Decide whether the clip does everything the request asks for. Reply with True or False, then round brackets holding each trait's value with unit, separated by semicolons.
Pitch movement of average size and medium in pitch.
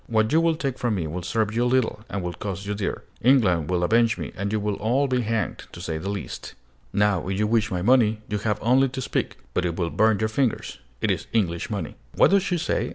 False (4.2 semitones; 110 Hz)